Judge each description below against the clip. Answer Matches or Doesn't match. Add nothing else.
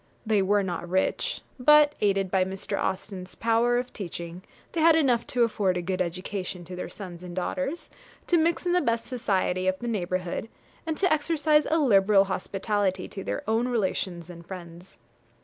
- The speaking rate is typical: Matches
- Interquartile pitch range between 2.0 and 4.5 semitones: Doesn't match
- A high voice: Matches